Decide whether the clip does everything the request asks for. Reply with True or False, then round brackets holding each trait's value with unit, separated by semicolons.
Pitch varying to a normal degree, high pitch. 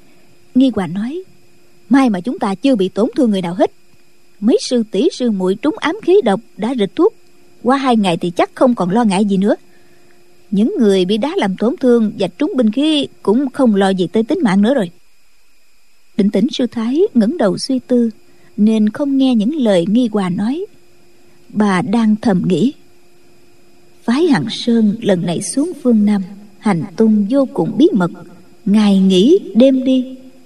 True (4.9 semitones; 230 Hz)